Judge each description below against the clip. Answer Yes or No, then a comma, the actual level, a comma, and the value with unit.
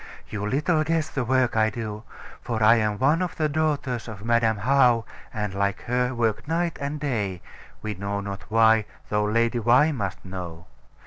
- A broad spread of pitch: No, average, 4.5 semitones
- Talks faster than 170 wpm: Yes, average, 180 wpm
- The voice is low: Yes, low, 115 Hz